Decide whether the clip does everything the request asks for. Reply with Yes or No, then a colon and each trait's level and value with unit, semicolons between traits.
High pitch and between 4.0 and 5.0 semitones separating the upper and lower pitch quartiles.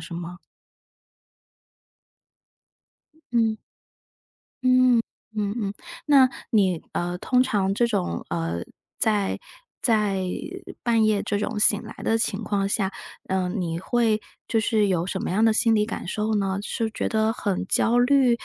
No: high, 210 Hz; average, 2.9 semitones